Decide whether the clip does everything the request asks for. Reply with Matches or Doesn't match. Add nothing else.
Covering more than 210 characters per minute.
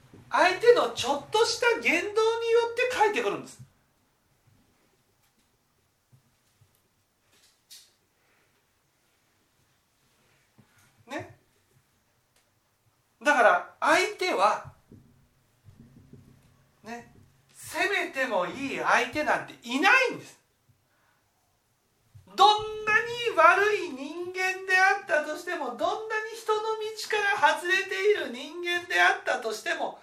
Doesn't match